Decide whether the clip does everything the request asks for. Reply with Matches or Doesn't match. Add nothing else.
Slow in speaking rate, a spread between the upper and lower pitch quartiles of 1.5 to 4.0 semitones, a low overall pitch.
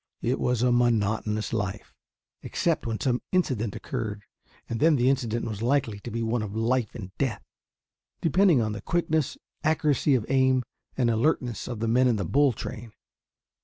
Doesn't match